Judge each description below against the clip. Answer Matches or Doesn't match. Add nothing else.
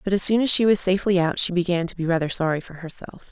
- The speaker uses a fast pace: Matches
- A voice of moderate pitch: Matches